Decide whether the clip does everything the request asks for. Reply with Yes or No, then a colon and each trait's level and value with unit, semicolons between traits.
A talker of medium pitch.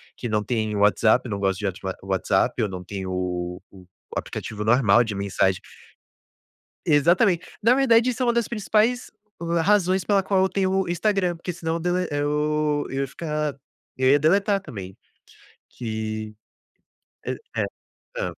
Yes: medium, 145 Hz